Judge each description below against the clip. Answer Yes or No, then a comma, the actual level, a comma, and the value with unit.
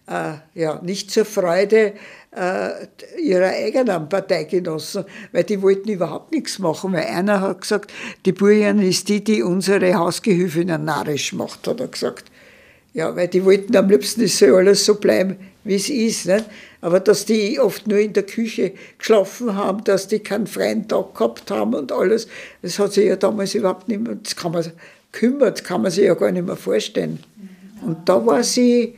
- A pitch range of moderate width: No, narrow, 2.2 semitones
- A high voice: Yes, high, 200 Hz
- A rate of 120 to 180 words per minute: No, fast, 190 wpm